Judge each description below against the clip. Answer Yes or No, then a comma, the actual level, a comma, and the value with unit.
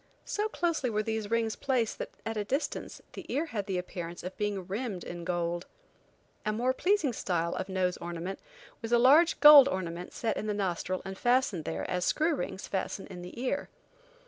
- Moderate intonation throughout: No, wide, 5.9 semitones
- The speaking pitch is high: Yes, high, 210 Hz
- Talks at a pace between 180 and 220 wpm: Yes, average, 195 wpm